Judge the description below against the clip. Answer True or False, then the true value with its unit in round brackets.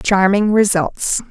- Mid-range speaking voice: False (200 Hz)